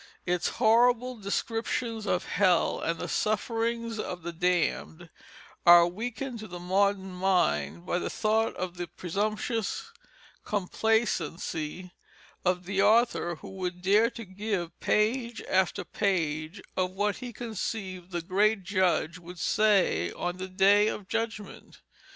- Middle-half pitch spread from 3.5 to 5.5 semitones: Yes, average, 3.8 semitones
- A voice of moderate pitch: No, high, 195 Hz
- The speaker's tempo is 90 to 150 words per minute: Yes, slow, 135 wpm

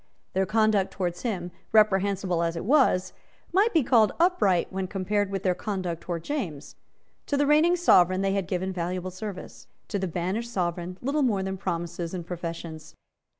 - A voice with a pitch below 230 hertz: Yes, high, 190 Hz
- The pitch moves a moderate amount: Yes, average, 3.5 semitones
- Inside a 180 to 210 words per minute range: No, average, 170 wpm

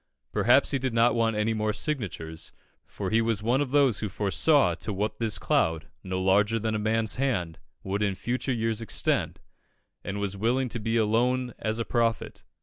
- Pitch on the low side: Yes, low, 110 Hz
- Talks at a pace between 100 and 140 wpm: No, average, 190 wpm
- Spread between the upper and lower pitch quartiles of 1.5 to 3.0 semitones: Yes, average, 2.7 semitones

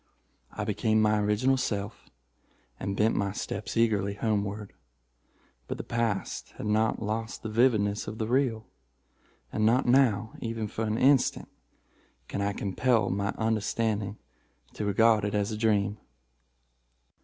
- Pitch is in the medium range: No, low, 110 Hz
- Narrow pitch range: Yes, narrow, 2.0 semitones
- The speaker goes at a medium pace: No, slow, 130 wpm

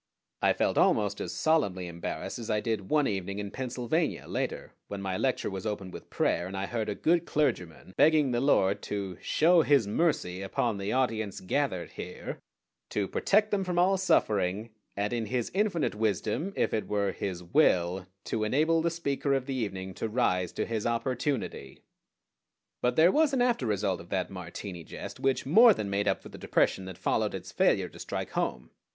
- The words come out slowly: No, average, 190 wpm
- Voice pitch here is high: No, low, 110 Hz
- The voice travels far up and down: Yes, wide, 7.2 semitones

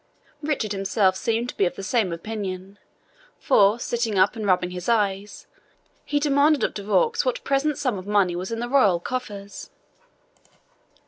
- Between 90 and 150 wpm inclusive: No, average, 170 wpm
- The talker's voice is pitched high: Yes, high, 210 Hz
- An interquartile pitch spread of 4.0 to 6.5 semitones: Yes, average, 4.7 semitones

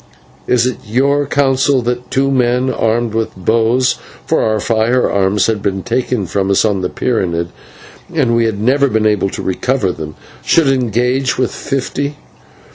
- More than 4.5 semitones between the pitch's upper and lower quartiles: No, average, 3.9 semitones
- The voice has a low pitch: Yes, low, 120 Hz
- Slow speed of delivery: No, average, 160 wpm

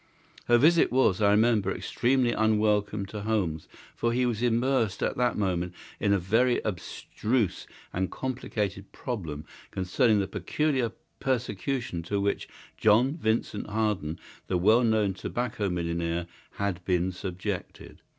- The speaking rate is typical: No, slow, 130 wpm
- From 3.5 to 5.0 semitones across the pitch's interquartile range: Yes, average, 4.2 semitones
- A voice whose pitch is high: No, low, 105 Hz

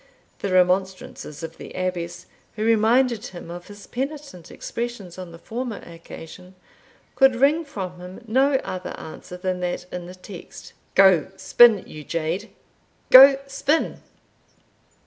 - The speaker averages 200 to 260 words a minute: No, slow, 135 wpm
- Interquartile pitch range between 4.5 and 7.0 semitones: Yes, average, 5.2 semitones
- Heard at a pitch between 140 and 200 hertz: Yes, high, 190 Hz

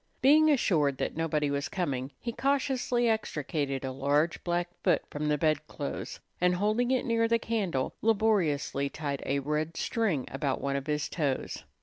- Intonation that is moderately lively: No, wide, 7.9 semitones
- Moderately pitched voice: Yes, medium, 155 Hz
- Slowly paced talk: No, average, 160 wpm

